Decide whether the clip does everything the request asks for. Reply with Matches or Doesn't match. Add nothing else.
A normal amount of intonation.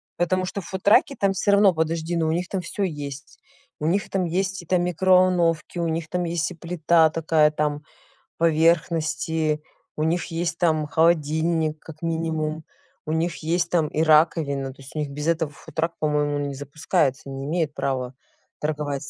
Doesn't match